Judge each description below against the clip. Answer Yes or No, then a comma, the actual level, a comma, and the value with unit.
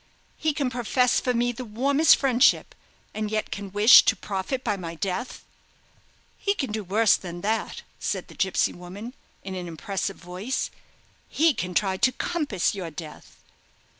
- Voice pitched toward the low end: No, high, 210 Hz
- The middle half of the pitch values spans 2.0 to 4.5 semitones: No, average, 5.1 semitones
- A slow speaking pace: No, average, 165 wpm